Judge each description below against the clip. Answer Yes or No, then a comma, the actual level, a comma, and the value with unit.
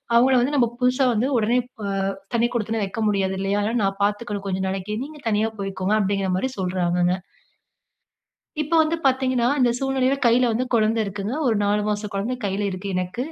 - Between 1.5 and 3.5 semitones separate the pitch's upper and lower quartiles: No, average, 4.2 semitones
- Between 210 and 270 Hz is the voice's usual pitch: Yes, high, 215 Hz